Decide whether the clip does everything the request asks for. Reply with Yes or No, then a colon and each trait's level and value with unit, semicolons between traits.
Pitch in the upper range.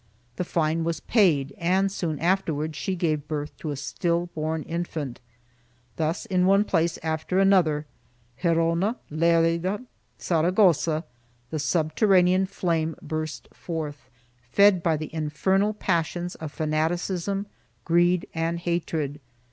No: medium, 165 Hz